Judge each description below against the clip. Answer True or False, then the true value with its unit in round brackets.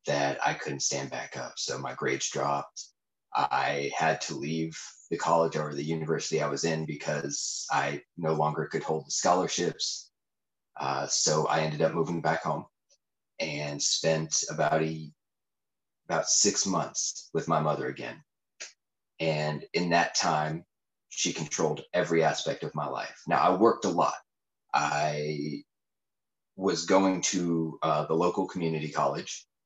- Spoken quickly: False (150 wpm)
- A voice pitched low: True (80 Hz)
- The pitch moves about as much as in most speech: False (1.6 semitones)